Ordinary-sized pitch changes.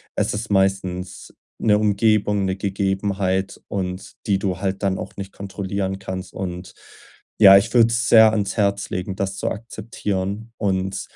No: narrow, 1.4 semitones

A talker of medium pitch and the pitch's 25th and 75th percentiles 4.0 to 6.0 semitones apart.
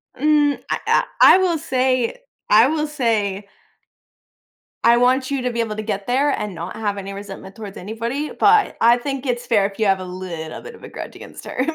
No: high, 235 Hz; average, 5.3 semitones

